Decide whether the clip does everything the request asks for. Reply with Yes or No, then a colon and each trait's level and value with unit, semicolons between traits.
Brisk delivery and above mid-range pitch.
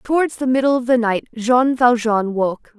No: average, 195 wpm; high, 240 Hz